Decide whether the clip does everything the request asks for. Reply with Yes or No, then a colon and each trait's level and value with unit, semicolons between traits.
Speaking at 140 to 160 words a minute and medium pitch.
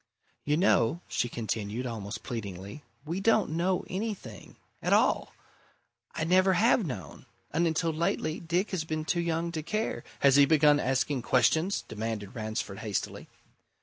Yes: average, 150 wpm; medium, 155 Hz